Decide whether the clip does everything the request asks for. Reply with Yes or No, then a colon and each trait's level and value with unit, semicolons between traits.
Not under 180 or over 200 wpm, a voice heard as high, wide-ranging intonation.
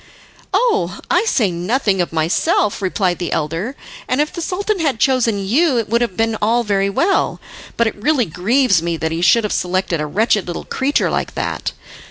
Yes: average, 195 wpm; high, 210 Hz; wide, 6.7 semitones